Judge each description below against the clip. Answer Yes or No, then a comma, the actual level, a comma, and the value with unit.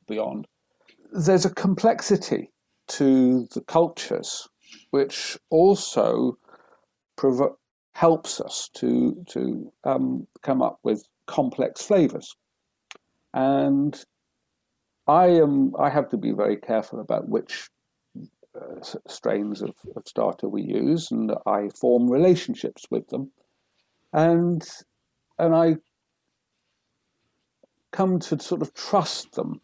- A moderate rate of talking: No, slow, 105 wpm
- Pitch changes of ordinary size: No, wide, 6.1 semitones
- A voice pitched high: No, medium, 165 Hz